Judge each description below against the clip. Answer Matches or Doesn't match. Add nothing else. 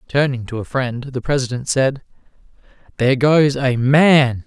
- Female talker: Doesn't match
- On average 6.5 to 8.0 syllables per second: Doesn't match